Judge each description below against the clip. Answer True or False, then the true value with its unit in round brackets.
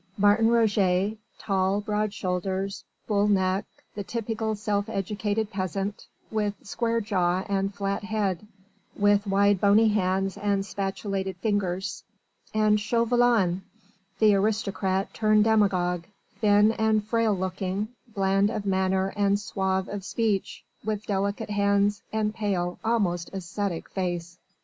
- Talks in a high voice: True (200 Hz)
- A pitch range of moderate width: False (2.0 semitones)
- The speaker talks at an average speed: False (120 wpm)